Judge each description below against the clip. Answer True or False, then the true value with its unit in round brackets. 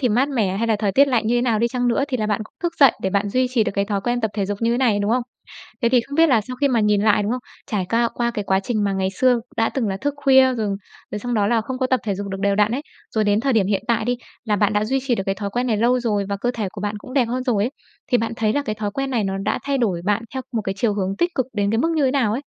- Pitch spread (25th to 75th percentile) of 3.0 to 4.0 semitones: True (3.6 semitones)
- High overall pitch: True (225 Hz)